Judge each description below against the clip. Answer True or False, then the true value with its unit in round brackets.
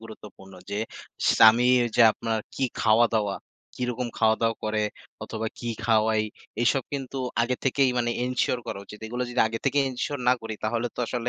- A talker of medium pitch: False (115 Hz)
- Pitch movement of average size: False (2.3 semitones)